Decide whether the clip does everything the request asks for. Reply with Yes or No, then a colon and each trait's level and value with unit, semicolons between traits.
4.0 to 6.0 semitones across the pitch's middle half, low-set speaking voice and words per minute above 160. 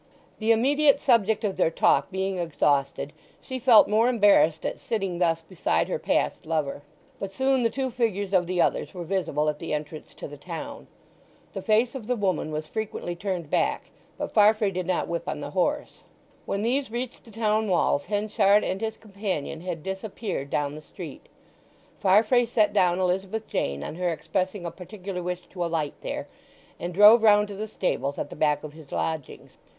No: average, 4.8 semitones; high, 190 Hz; average, 185 wpm